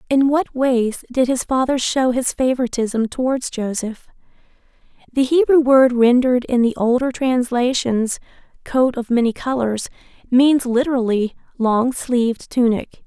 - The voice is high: Yes, very high, 250 Hz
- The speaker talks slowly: Yes, slow, 130 wpm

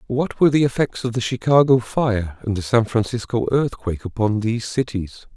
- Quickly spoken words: No, average, 180 wpm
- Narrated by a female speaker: No, male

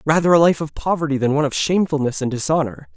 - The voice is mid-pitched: Yes, medium, 150 Hz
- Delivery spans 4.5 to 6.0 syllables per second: No, 7.1 syllables/s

